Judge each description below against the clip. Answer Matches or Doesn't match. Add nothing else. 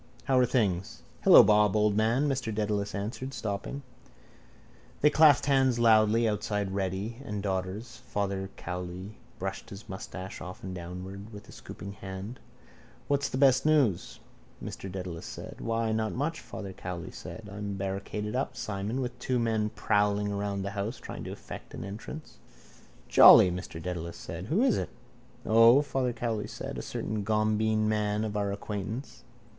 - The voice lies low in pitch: Matches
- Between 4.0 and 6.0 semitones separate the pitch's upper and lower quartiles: Doesn't match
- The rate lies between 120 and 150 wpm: Doesn't match